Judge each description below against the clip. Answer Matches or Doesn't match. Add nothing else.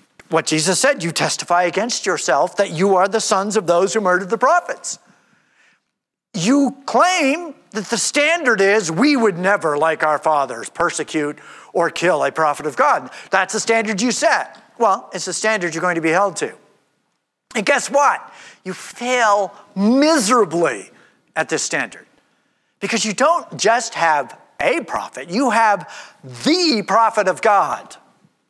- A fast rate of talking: Doesn't match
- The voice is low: Doesn't match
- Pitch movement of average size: Doesn't match